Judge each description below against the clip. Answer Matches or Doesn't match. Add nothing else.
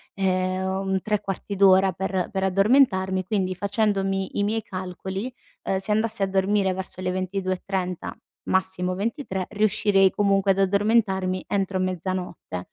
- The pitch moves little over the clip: Matches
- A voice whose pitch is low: Doesn't match